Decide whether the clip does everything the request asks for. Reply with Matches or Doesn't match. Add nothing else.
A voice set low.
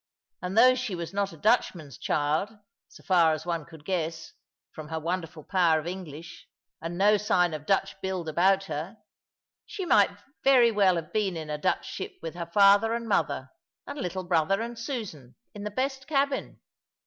Doesn't match